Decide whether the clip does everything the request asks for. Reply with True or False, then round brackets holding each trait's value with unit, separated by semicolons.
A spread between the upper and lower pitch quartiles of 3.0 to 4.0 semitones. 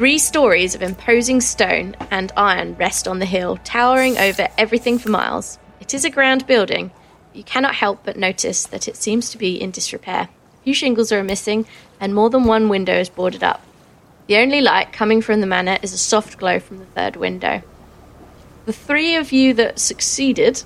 False (4.8 semitones)